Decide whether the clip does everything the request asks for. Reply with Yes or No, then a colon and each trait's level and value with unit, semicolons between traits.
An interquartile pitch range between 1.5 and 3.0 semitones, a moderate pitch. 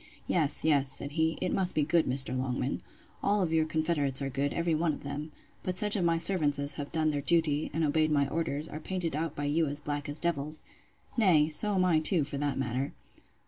Yes: average, 2.7 semitones; medium, 155 Hz